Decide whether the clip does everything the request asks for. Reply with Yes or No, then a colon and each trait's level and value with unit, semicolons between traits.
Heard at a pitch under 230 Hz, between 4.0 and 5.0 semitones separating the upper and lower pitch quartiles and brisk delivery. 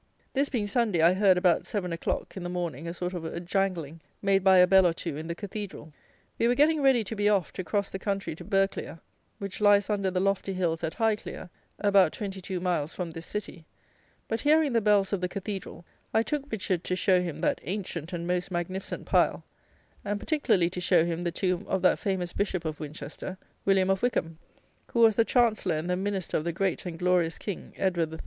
No: medium, 185 Hz; average, 2.9 semitones; fast, 215 wpm